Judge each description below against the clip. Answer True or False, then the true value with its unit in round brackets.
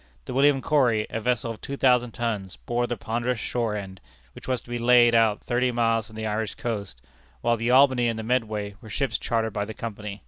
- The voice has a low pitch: True (115 Hz)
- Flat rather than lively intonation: True (2.2 semitones)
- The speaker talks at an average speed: False (220 wpm)